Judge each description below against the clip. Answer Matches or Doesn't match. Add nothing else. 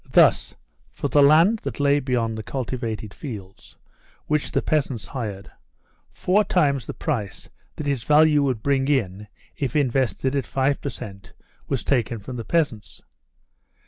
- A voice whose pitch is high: Doesn't match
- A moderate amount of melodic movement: Matches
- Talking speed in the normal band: Matches